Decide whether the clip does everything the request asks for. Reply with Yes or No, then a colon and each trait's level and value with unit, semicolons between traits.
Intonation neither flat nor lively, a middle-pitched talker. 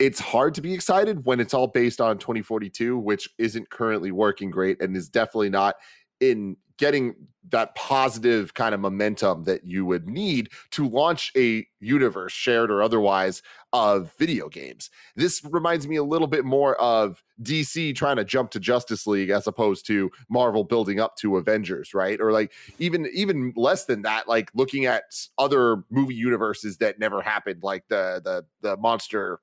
No: average, 4.2 semitones; low, 115 Hz